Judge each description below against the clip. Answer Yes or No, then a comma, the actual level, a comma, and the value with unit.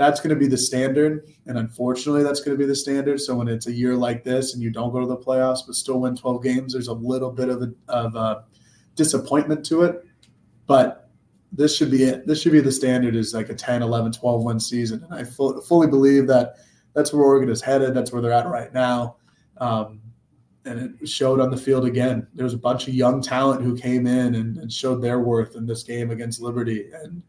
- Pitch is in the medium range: No, low, 125 Hz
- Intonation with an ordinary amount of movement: No, narrow, 2.3 semitones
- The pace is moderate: No, fast, 235 wpm